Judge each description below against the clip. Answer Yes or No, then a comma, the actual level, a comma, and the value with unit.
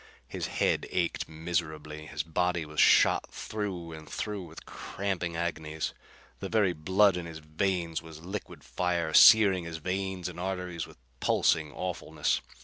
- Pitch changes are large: No, average, 2.8 semitones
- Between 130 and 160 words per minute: Yes, average, 145 wpm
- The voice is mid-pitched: No, very low, 85 Hz